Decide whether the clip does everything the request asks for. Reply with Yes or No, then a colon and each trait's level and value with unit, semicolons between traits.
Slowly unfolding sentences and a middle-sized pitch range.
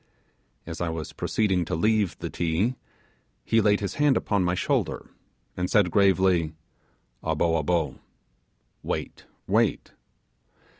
Yes: slow, 120 wpm; average, 3.8 semitones